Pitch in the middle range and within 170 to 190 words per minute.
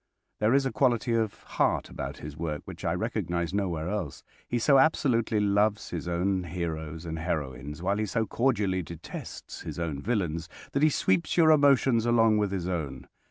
No: very low, 95 Hz; average, 180 wpm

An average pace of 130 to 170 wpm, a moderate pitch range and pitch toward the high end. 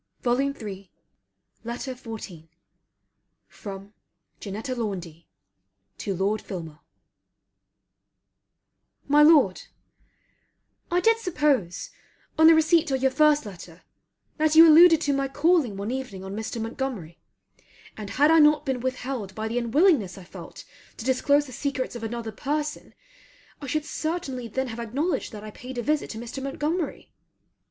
No: average, 140 wpm; wide, 5.8 semitones; very high, 255 Hz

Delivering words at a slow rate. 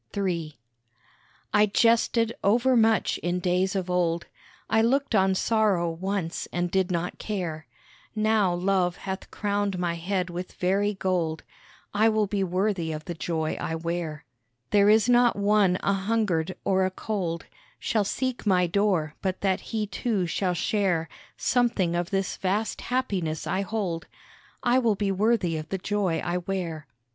No: average, 155 wpm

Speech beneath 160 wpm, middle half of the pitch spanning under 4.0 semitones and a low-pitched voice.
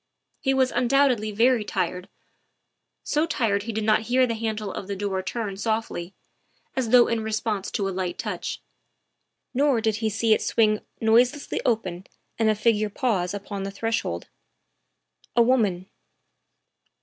No: average, 150 wpm; average, 2.9 semitones; high, 220 Hz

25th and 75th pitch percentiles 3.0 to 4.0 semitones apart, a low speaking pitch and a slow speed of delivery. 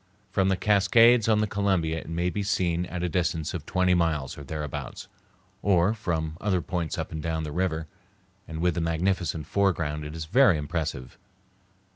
No: average, 3.3 semitones; very low, 85 Hz; average, 180 wpm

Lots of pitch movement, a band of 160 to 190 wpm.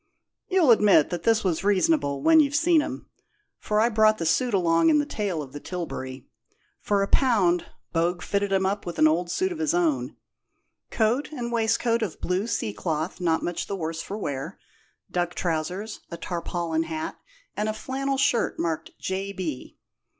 Yes: wide, 5.9 semitones; average, 180 wpm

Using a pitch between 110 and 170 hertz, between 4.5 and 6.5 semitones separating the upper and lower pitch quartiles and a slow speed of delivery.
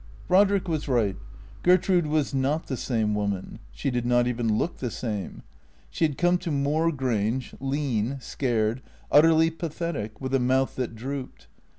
No: low, 135 Hz; average, 5.1 semitones; average, 160 wpm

